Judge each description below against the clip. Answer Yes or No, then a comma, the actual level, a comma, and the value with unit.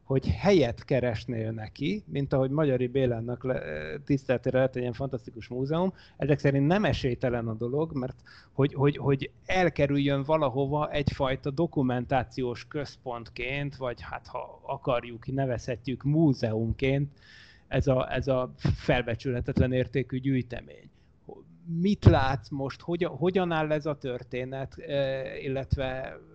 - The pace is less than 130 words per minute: Yes, average, 115 wpm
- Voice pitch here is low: Yes, low, 130 Hz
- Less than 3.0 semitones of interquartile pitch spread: Yes, narrow, 2.4 semitones